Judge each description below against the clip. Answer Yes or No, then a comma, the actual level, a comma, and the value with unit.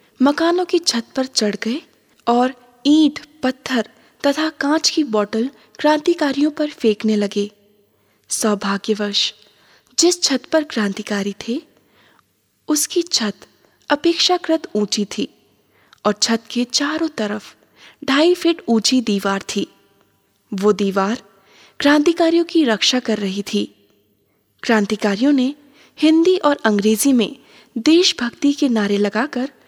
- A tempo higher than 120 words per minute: No, average, 115 wpm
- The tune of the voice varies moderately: No, wide, 6.4 semitones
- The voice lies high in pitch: Yes, high, 245 Hz